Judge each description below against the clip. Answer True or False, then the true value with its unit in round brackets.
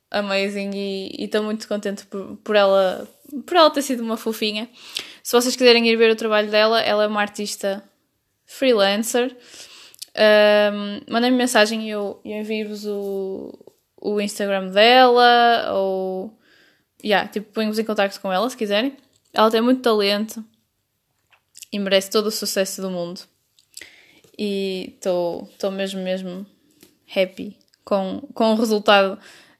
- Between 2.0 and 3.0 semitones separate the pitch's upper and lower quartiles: True (2.6 semitones)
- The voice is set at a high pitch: True (210 Hz)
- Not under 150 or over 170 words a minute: False (140 wpm)